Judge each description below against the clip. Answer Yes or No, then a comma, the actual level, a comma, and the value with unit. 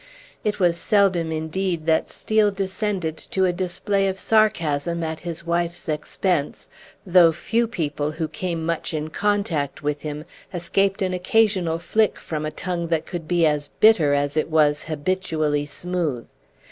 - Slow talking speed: No, average, 155 wpm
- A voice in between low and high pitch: Yes, medium, 170 Hz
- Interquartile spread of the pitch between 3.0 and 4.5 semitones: Yes, average, 3.4 semitones